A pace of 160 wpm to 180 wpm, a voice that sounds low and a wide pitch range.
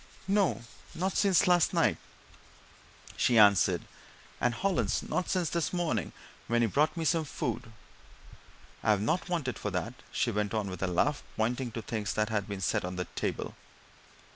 Yes: average, 165 wpm; low, 120 Hz; wide, 8.4 semitones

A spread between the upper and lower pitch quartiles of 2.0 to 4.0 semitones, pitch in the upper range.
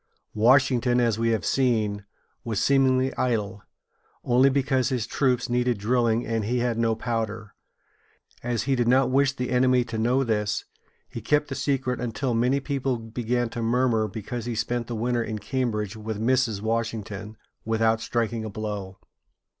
No: narrow, 2.4 semitones; low, 120 Hz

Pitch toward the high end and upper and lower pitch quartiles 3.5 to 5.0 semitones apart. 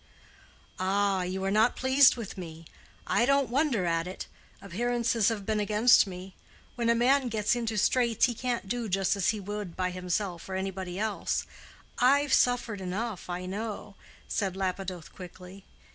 Yes: high, 205 Hz; average, 4.1 semitones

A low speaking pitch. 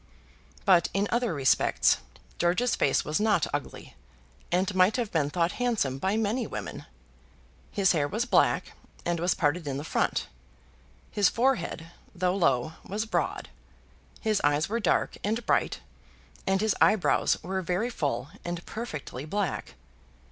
No: medium, 185 Hz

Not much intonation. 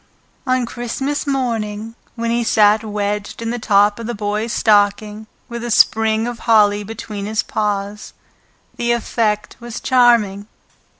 Yes: narrow, 2.3 semitones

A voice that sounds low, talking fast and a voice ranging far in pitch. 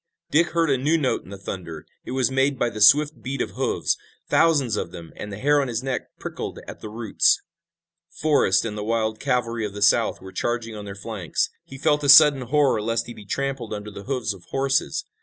No: low, 120 Hz; fast, 225 wpm; average, 4.7 semitones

